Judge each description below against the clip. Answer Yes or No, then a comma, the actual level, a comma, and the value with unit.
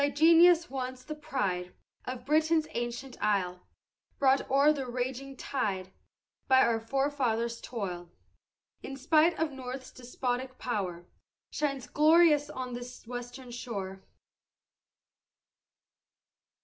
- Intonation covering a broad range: No, average, 3.4 semitones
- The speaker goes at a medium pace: No, slow, 110 wpm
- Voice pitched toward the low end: No, very high, 255 Hz